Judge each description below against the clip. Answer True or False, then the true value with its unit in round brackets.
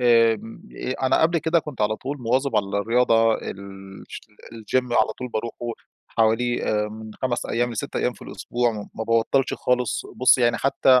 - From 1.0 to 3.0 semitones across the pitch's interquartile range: True (2.5 semitones)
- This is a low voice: True (115 Hz)